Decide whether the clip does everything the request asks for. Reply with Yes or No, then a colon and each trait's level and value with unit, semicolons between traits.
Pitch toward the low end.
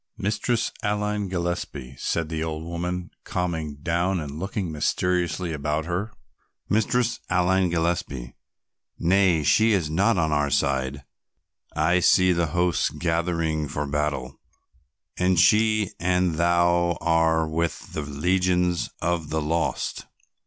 Yes: very low, 85 Hz